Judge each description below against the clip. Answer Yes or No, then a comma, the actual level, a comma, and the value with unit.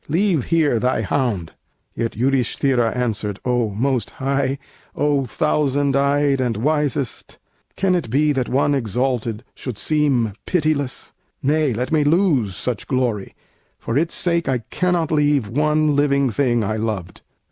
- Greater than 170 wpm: No, average, 140 wpm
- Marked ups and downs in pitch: No, average, 4.0 semitones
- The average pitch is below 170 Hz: Yes, low, 135 Hz